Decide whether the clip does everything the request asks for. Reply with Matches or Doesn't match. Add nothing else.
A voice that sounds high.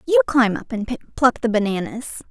Matches